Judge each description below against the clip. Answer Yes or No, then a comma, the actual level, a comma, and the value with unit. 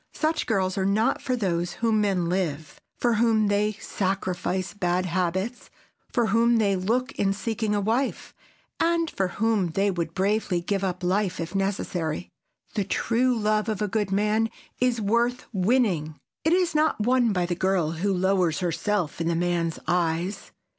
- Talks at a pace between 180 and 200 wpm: No, average, 165 wpm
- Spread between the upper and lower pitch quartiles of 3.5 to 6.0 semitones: Yes, average, 3.8 semitones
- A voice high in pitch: Yes, high, 200 Hz